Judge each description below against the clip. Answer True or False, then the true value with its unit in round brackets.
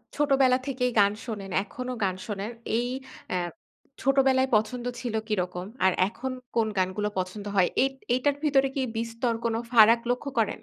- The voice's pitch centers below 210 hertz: False (230 Hz)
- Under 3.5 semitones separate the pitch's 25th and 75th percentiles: False (4.1 semitones)